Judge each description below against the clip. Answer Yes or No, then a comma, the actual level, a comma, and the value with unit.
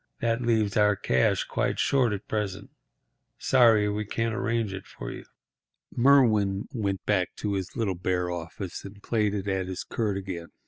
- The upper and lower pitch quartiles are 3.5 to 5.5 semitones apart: No, average, 3.1 semitones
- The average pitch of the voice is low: Yes, low, 105 Hz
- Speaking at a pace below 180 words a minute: Yes, average, 165 wpm